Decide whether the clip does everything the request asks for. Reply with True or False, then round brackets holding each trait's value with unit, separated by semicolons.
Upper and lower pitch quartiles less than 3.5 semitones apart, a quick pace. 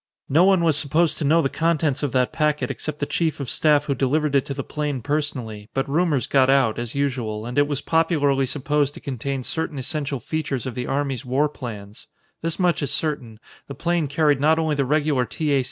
True (2.7 semitones; 220 wpm)